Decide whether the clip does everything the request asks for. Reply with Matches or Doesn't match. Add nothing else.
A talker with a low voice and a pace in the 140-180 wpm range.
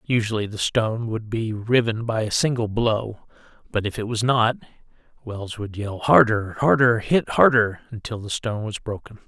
Matches